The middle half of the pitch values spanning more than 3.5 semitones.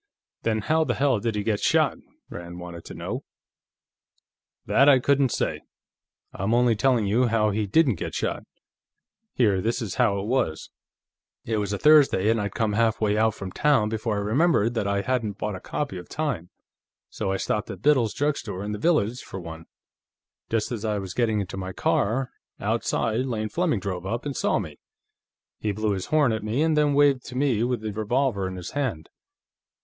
Yes: average, 4.3 semitones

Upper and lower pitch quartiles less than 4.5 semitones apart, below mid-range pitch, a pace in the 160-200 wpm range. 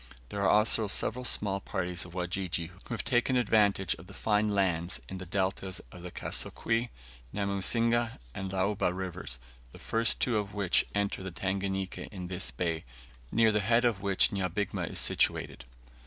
Yes: narrow, 2.5 semitones; low, 100 Hz; average, 170 wpm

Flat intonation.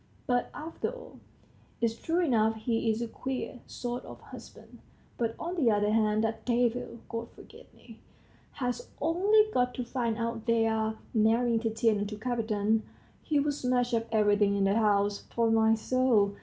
Yes: narrow, 2.2 semitones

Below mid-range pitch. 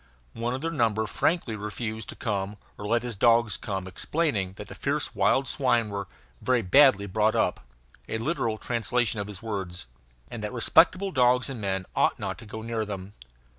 Yes: low, 110 Hz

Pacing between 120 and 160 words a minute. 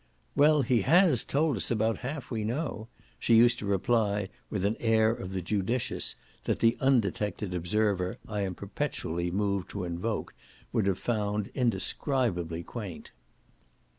Yes: average, 145 wpm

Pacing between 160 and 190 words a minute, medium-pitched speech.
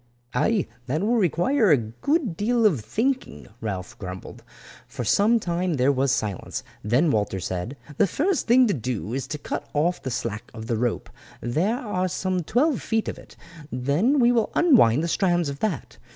Yes: average, 180 wpm; medium, 165 Hz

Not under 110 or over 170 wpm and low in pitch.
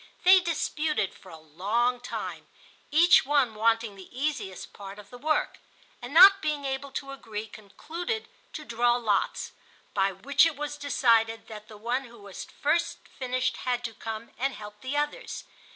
No: average, 160 wpm; high, 245 Hz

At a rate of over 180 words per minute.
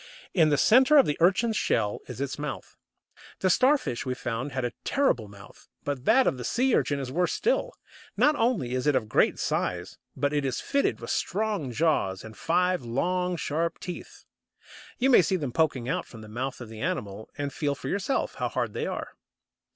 Yes: average, 195 wpm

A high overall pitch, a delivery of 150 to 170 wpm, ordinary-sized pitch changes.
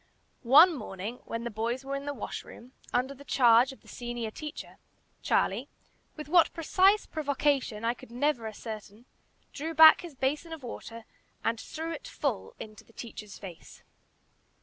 Yes: very high, 255 Hz; average, 160 wpm; average, 4.8 semitones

